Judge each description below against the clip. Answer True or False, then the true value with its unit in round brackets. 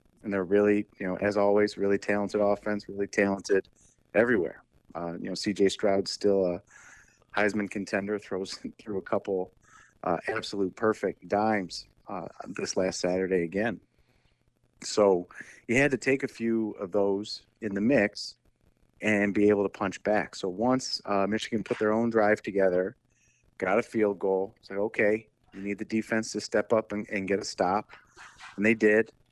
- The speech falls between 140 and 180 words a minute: True (170 wpm)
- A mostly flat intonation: True (1.9 semitones)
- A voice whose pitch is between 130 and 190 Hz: False (105 Hz)